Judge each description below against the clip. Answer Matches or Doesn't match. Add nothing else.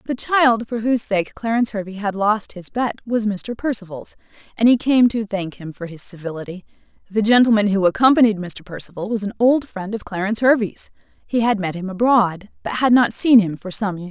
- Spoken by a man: Doesn't match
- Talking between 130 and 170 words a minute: Doesn't match